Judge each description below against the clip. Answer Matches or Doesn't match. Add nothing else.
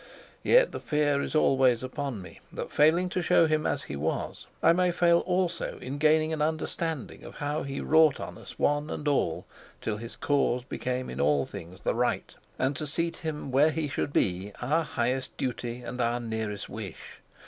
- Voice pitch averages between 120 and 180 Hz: Matches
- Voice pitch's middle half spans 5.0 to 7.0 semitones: Doesn't match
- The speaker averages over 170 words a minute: Matches